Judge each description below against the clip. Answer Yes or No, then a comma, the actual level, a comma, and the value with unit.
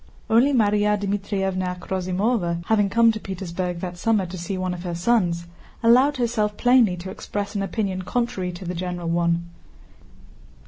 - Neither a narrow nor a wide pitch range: Yes, average, 3.6 semitones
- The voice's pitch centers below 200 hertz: Yes, high, 190 Hz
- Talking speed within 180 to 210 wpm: No, average, 165 wpm